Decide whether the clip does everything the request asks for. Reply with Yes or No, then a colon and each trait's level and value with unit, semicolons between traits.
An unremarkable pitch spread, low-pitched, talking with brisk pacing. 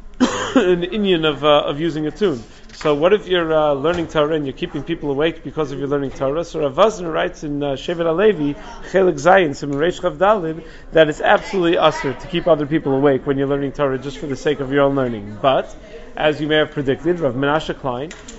No: average, 3.4 semitones; medium, 155 Hz; fast, 215 wpm